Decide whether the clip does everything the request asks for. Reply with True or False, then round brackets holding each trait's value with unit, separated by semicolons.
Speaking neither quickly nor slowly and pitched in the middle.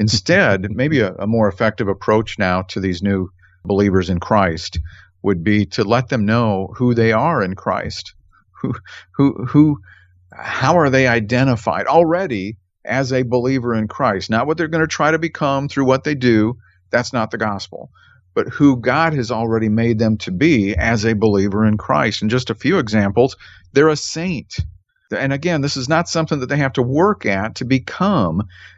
False (190 wpm; 115 Hz)